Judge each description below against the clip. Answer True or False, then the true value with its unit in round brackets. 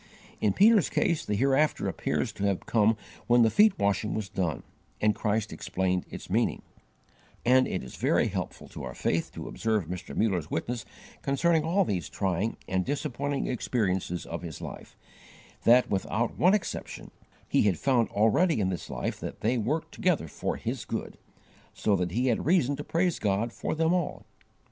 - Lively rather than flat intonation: True (7.3 semitones)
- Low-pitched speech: True (115 Hz)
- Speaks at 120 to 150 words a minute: False (175 wpm)